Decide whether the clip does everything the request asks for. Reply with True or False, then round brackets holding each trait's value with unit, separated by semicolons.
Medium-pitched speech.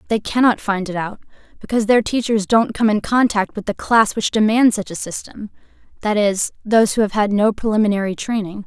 False (210 Hz)